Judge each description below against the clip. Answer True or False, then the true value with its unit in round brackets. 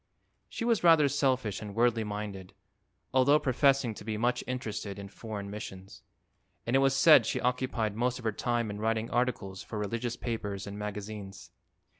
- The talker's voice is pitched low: True (115 Hz)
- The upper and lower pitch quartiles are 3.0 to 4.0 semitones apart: True (3.6 semitones)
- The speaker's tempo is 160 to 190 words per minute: True (170 wpm)